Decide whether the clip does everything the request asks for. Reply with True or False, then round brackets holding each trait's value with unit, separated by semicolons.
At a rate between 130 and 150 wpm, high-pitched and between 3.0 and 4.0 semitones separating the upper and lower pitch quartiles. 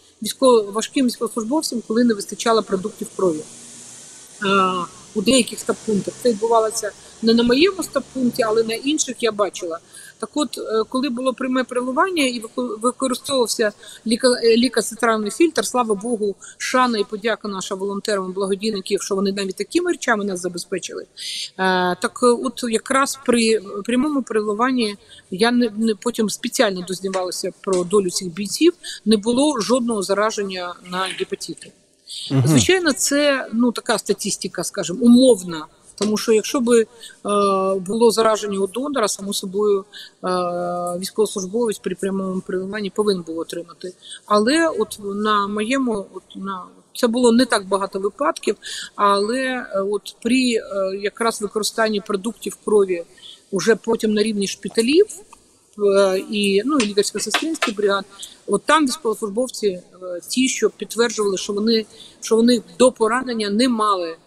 True (135 wpm; 215 Hz; 3.6 semitones)